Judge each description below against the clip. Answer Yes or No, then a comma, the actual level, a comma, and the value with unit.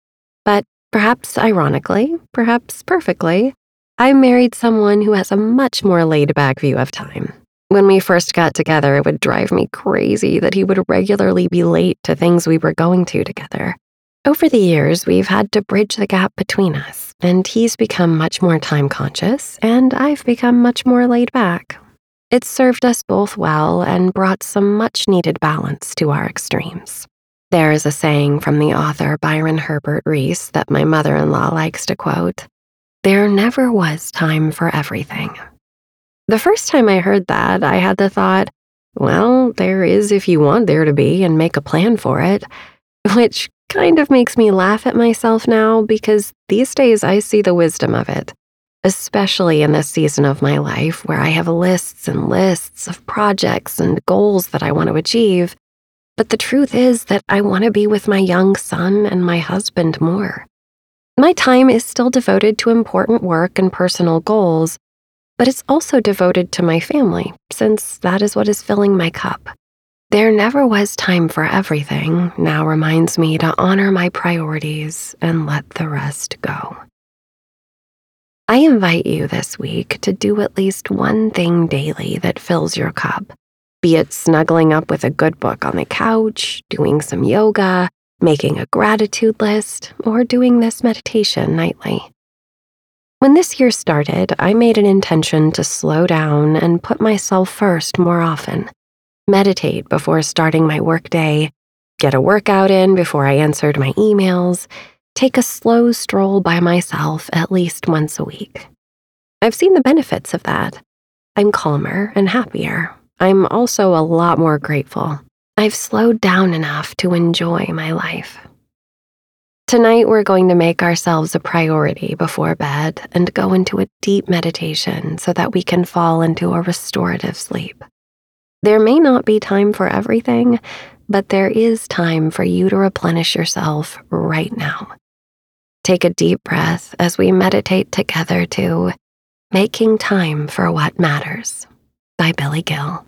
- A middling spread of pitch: Yes, average, 5.0 semitones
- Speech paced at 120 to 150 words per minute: No, average, 165 wpm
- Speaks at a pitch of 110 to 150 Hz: No, medium, 185 Hz